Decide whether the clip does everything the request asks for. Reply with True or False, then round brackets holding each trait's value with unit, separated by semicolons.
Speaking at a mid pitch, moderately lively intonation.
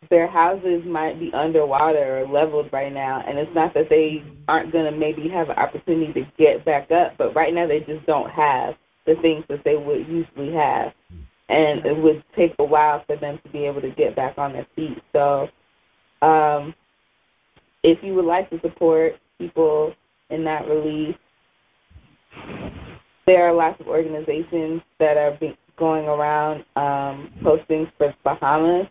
False (155 Hz; 1.9 semitones)